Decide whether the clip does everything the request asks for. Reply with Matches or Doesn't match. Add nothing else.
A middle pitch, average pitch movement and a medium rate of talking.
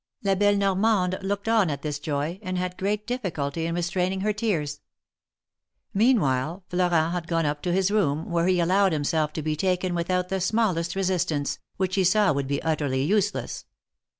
Matches